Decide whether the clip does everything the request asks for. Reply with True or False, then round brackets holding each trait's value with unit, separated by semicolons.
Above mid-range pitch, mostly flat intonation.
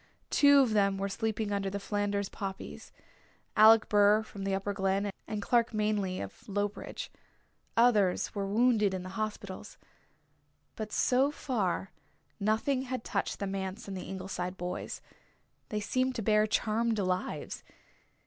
True (205 Hz; 2.2 semitones)